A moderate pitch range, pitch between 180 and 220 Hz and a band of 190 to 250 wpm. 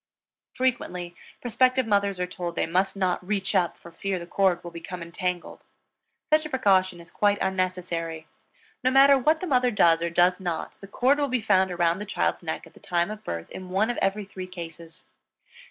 Yes: average, 3.5 semitones; medium, 185 Hz; average, 200 wpm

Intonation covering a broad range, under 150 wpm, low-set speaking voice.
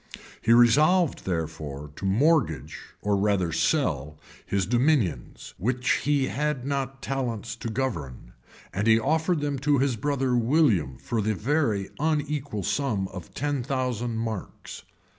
Yes: wide, 6.4 semitones; average, 140 wpm; low, 120 Hz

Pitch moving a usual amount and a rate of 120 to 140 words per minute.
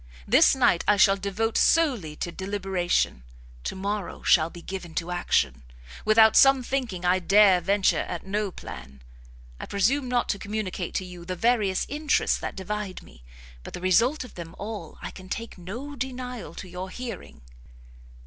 No: average, 4.3 semitones; average, 170 wpm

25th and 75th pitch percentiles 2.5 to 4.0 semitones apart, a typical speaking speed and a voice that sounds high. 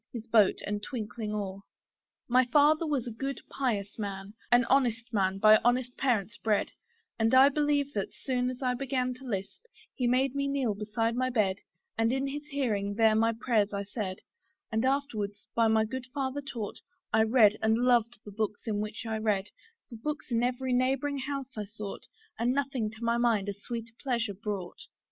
Yes: average, 3.5 semitones; average, 190 wpm; high, 230 Hz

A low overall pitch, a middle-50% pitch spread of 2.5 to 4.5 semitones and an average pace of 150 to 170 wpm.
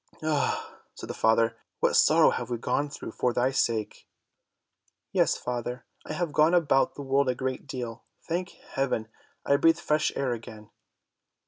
Yes: low, 130 Hz; average, 3.7 semitones; average, 160 wpm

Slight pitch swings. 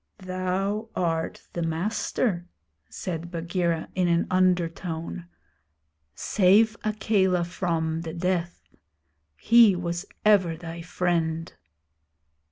Yes: narrow, 2.2 semitones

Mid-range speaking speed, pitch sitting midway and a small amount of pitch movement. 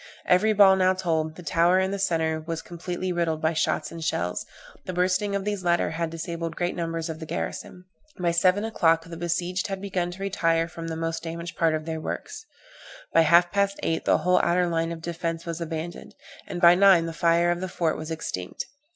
No: fast, 210 wpm; medium, 170 Hz; narrow, 1.8 semitones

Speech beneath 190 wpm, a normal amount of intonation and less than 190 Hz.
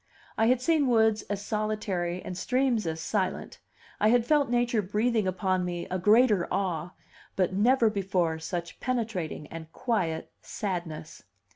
No: average, 145 wpm; average, 4.6 semitones; high, 200 Hz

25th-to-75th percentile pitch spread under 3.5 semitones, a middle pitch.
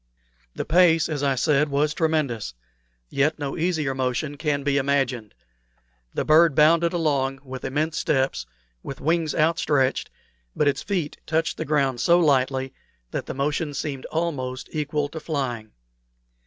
Yes: average, 2.9 semitones; medium, 145 Hz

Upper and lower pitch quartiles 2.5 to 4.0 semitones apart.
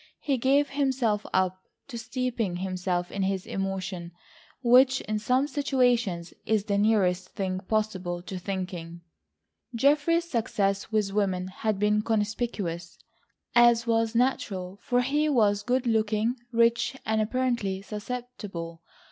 No: average, 4.5 semitones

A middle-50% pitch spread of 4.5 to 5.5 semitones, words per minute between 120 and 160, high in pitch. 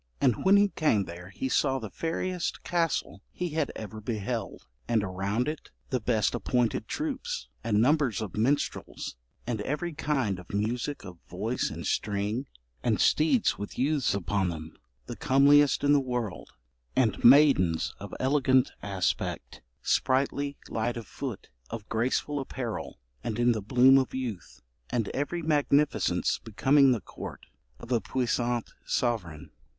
No: average, 5.2 semitones; average, 145 wpm; low, 125 Hz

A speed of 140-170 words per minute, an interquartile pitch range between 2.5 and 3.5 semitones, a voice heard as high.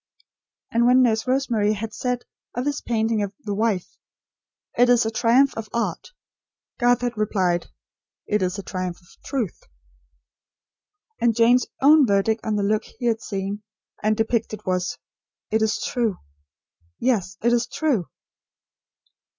Yes: average, 145 wpm; average, 2.9 semitones; high, 225 Hz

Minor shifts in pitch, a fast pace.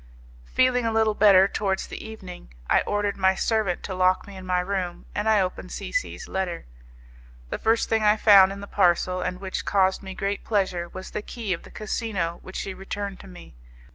Yes: narrow, 2.2 semitones; fast, 210 wpm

